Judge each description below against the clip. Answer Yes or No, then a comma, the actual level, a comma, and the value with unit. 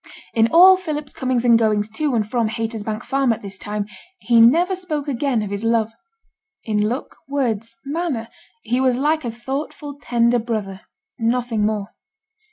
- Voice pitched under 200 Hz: No, high, 235 Hz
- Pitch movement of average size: Yes, average, 4.0 semitones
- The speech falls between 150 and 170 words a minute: Yes, average, 165 wpm